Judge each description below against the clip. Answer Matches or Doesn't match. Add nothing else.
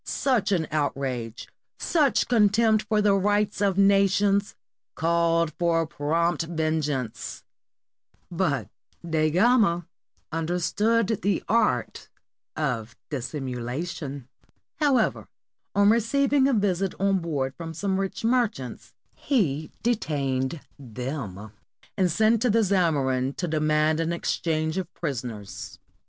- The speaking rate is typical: Doesn't match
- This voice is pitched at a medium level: Matches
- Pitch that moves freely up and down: Matches